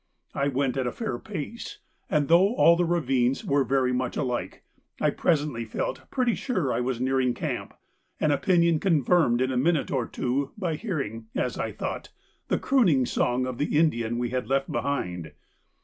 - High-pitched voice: No, low, 135 Hz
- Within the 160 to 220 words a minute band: Yes, average, 180 wpm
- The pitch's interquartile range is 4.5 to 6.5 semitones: Yes, average, 5.2 semitones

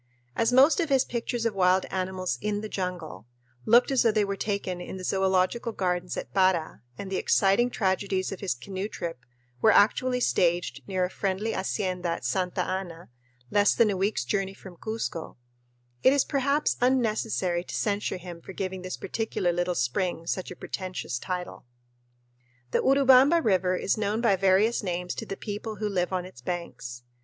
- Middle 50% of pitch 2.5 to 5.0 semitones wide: Yes, average, 3.3 semitones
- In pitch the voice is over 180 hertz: Yes, high, 190 Hz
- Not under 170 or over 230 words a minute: Yes, average, 180 wpm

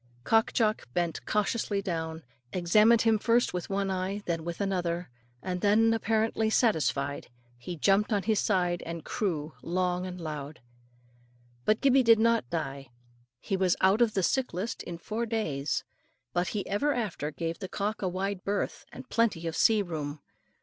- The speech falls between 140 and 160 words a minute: No, average, 170 wpm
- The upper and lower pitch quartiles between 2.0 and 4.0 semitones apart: No, average, 4.5 semitones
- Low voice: No, high, 190 Hz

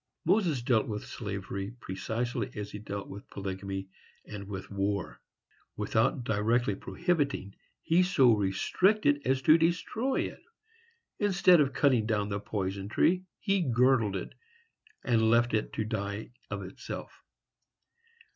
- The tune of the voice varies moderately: No, wide, 5.9 semitones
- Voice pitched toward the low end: Yes, low, 110 Hz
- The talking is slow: Yes, slow, 130 wpm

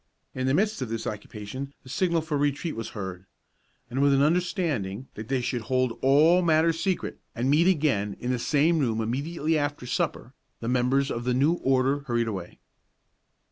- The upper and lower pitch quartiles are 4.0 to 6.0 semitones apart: Yes, average, 4.8 semitones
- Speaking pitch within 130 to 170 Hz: Yes, low, 135 Hz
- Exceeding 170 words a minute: Yes, average, 180 wpm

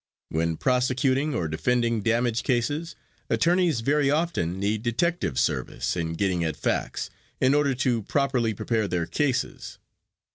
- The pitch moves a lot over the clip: Yes, wide, 6.1 semitones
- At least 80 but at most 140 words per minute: Yes, slow, 135 wpm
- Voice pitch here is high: No, low, 120 Hz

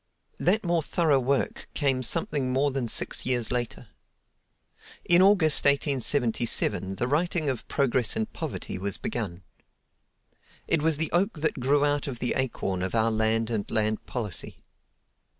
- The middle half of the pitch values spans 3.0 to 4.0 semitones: No, average, 4.7 semitones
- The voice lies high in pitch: No, low, 130 Hz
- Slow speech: No, average, 150 wpm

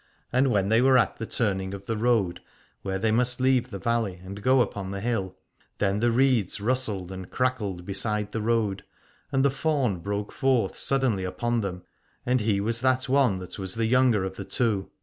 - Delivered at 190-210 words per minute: Yes, average, 200 wpm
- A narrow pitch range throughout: No, average, 4.3 semitones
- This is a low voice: Yes, low, 110 Hz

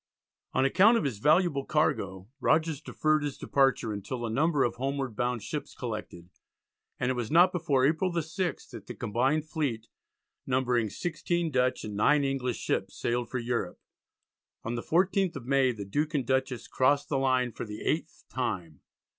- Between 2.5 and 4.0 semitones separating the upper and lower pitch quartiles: No, average, 4.5 semitones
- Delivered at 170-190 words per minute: Yes, average, 175 wpm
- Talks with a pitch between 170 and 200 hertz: No, low, 135 Hz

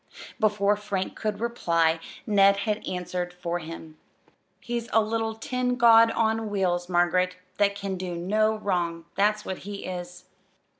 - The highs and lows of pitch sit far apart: No, average, 3.5 semitones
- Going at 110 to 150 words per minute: Yes, average, 145 wpm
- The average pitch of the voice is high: Yes, high, 200 Hz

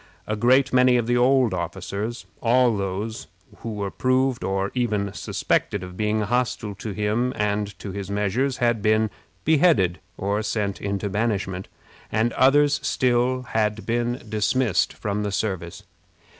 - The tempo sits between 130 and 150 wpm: Yes, average, 145 wpm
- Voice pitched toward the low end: Yes, low, 110 Hz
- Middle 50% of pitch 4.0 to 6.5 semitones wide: No, average, 3.5 semitones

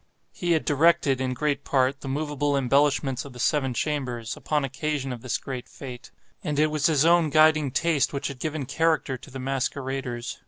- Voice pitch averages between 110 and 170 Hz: Yes, medium, 140 Hz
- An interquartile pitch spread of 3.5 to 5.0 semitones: No, narrow, 2.5 semitones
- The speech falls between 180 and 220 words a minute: Yes, average, 190 wpm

